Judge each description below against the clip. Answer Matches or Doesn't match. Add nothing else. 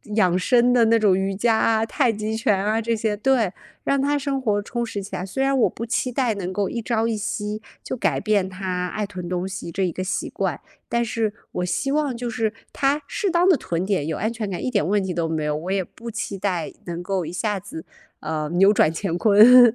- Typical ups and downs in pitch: Matches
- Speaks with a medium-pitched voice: Doesn't match